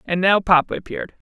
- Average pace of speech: Yes, average, 185 wpm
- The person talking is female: Yes, female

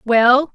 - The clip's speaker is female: Yes, female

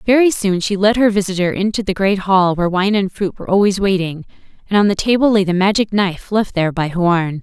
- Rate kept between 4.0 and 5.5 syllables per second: No, 6.0 syllables/s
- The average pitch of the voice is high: Yes, high, 195 Hz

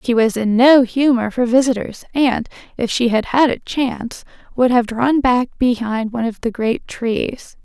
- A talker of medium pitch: No, high, 240 Hz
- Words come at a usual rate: Yes, average, 190 wpm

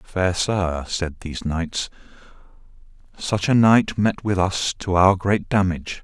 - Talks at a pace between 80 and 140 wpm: No, average, 150 wpm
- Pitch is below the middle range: Yes, very low, 95 Hz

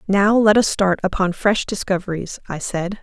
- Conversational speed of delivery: Yes, average, 180 wpm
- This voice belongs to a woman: Yes, female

